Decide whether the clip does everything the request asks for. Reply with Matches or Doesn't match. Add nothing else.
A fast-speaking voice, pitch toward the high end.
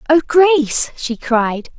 Doesn't match